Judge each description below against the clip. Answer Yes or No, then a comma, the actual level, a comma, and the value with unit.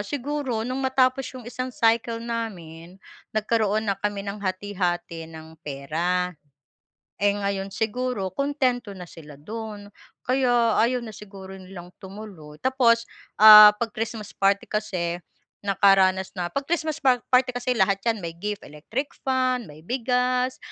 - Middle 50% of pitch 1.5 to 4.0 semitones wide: No, average, 4.7 semitones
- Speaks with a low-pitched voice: No, high, 210 Hz